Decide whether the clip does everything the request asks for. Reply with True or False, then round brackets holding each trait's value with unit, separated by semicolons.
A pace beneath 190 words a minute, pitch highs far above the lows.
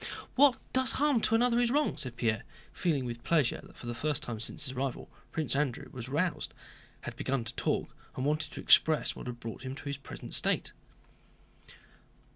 False (195 wpm; 5.7 semitones)